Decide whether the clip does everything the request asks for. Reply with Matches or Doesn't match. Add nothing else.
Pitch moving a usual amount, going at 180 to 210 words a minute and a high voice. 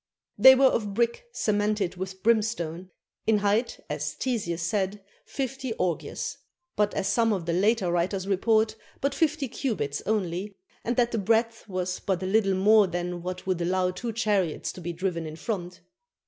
Doesn't match